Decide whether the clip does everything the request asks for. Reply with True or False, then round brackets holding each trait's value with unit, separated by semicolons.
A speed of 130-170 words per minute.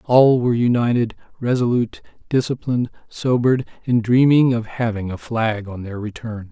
True (140 wpm)